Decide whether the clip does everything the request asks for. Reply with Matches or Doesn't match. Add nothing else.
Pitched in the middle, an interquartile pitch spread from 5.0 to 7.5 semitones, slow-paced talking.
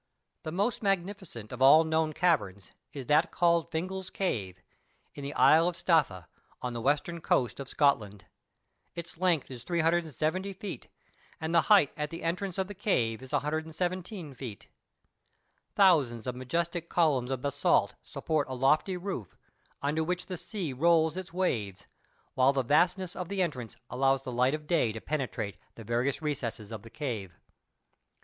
Doesn't match